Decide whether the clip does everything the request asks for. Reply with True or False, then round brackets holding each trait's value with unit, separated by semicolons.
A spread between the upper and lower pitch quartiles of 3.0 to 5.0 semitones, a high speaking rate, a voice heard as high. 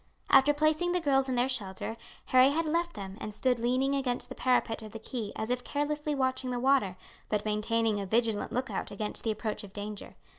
True (4.2 semitones; 215 wpm; 245 Hz)